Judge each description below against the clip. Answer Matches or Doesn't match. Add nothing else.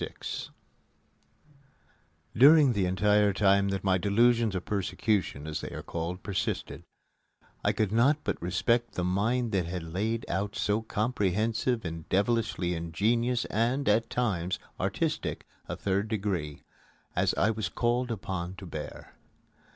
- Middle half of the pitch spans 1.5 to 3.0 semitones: Doesn't match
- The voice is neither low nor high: Doesn't match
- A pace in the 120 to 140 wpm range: Matches